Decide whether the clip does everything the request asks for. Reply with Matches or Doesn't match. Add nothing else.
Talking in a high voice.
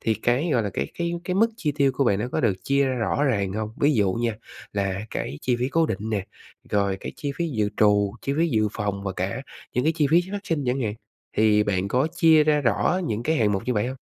Doesn't match